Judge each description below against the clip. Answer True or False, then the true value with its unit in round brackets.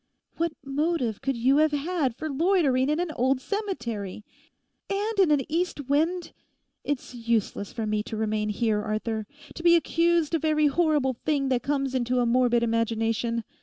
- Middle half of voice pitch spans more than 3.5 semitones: True (5.4 semitones)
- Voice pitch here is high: True (270 Hz)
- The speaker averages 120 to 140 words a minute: False (165 wpm)